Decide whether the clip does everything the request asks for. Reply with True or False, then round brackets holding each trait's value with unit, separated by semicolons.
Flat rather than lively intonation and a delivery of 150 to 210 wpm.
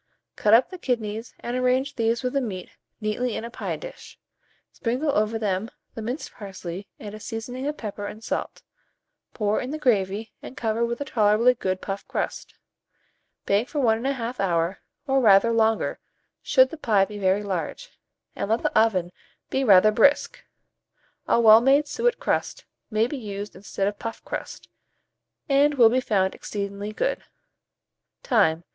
False (3.7 semitones; 165 wpm)